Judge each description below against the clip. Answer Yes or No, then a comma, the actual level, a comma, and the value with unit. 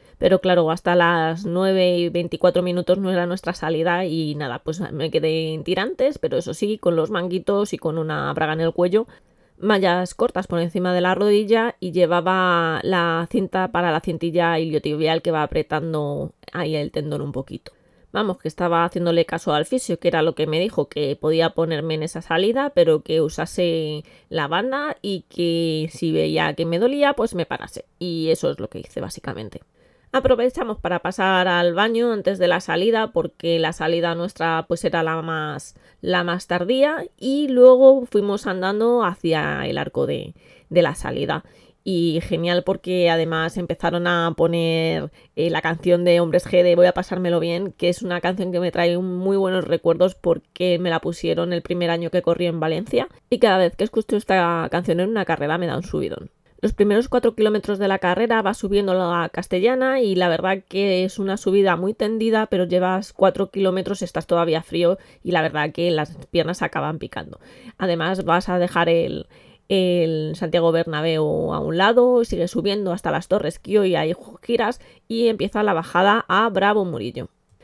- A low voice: No, medium, 175 Hz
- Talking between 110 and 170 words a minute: No, fast, 190 wpm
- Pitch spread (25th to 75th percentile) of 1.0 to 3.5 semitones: Yes, average, 2.7 semitones